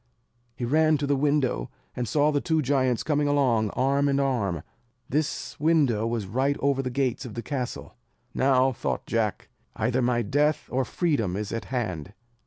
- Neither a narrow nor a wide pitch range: Yes, average, 3.4 semitones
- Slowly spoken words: No, average, 175 wpm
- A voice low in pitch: Yes, low, 130 Hz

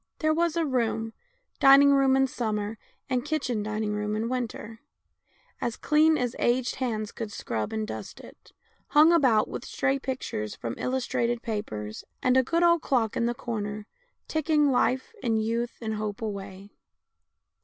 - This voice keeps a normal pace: Yes, average, 160 wpm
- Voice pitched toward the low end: No, high, 235 Hz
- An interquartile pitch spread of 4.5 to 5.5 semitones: No, average, 4.1 semitones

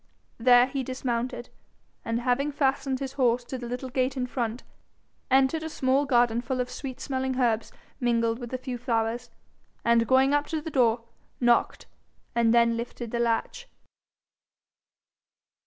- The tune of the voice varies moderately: No, narrow, 2.0 semitones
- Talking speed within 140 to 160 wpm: Yes, average, 155 wpm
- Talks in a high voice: Yes, very high, 250 Hz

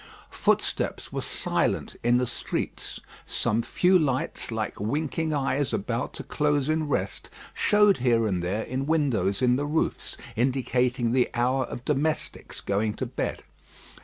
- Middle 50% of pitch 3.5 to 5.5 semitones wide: Yes, average, 4.1 semitones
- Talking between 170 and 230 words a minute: No, average, 145 wpm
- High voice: No, low, 130 Hz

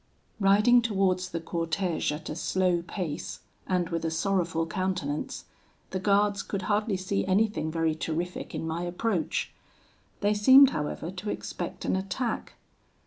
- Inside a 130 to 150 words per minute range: Yes, average, 140 wpm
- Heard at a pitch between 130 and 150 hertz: No, medium, 185 Hz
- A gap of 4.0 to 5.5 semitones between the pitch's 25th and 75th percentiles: No, average, 3.5 semitones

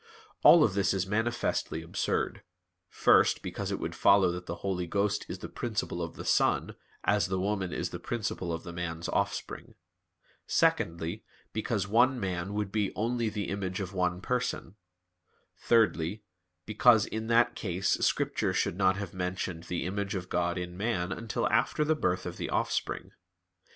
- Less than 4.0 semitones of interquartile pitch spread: Yes, average, 3.4 semitones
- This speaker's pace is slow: No, average, 165 wpm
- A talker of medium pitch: No, very low, 95 Hz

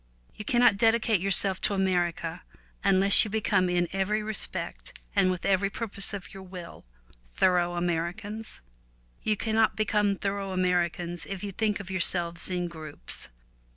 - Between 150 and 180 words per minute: Yes, average, 155 wpm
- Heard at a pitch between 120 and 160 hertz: No, high, 190 Hz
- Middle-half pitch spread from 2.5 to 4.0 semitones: Yes, average, 2.8 semitones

